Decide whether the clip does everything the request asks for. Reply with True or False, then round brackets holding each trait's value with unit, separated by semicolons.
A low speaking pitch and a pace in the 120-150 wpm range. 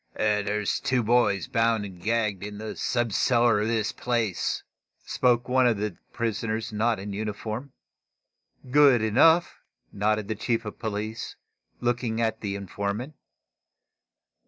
True (110 Hz; 135 wpm)